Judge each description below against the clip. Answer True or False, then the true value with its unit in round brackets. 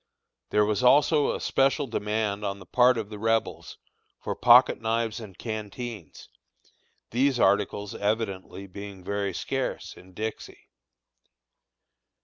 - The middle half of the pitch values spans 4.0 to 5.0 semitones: False (2.8 semitones)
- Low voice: True (110 Hz)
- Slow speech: True (125 wpm)